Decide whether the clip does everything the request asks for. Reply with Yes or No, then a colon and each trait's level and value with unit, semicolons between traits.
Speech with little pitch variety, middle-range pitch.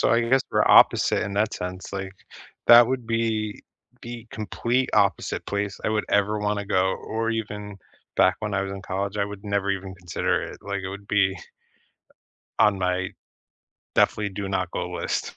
No: narrow, 2.0 semitones; low, 100 Hz